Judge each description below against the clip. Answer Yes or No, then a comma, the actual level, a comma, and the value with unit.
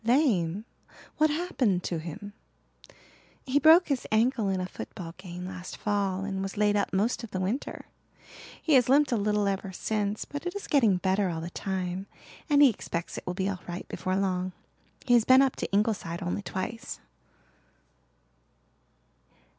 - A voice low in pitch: No, high, 200 Hz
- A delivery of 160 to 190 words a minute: Yes, average, 170 wpm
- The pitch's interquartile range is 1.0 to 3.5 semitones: No, average, 4.8 semitones